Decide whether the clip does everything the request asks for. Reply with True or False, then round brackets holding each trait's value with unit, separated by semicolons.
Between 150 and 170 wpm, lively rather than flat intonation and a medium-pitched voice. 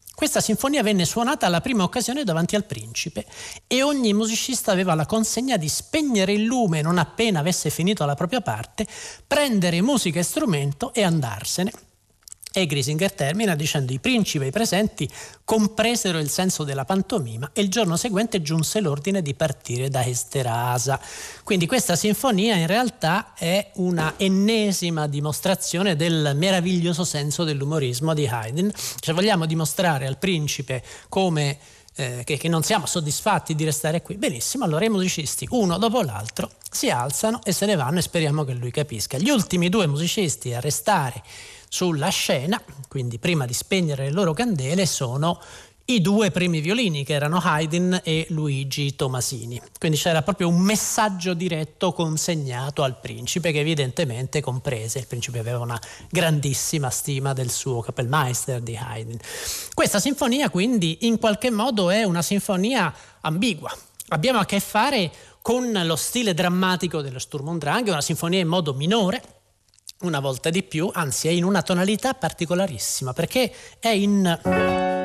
True (155 wpm; 6.1 semitones; 170 Hz)